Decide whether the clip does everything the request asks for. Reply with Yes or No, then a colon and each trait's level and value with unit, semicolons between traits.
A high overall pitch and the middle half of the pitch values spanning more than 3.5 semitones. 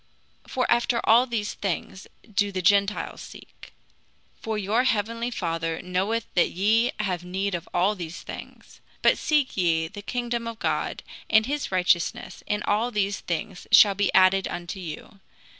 Yes: high, 200 Hz; average, 3.9 semitones